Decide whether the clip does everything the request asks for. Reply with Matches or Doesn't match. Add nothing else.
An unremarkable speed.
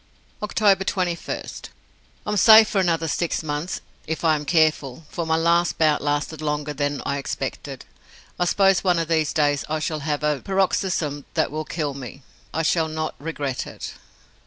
Matches